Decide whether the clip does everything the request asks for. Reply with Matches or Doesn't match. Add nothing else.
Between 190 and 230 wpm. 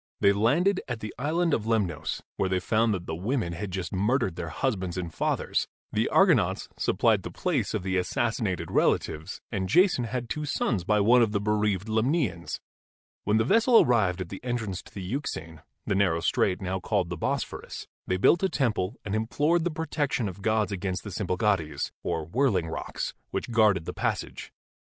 Matches